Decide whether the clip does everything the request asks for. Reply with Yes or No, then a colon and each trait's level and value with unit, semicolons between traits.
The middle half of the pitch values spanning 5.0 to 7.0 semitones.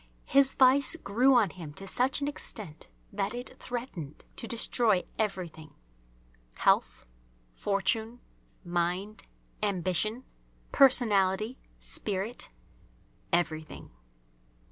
Yes: wide, 5.4 semitones